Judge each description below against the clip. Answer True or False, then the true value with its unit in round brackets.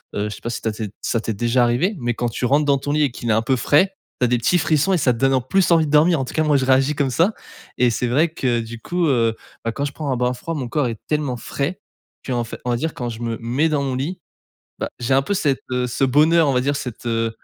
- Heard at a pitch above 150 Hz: False (130 Hz)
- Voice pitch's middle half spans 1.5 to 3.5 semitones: False (4.0 semitones)